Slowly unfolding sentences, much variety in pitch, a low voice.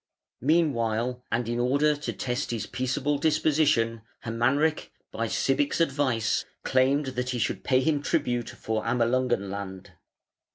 No: slow, 130 wpm; average, 3.7 semitones; low, 125 Hz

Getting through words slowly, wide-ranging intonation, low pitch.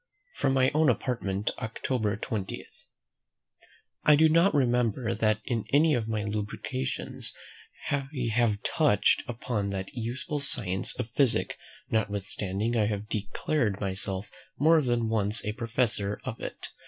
No: slow, 130 wpm; average, 3.9 semitones; low, 115 Hz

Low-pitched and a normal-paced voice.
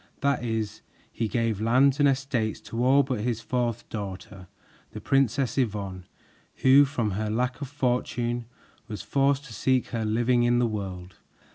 Yes: low, 120 Hz; average, 160 wpm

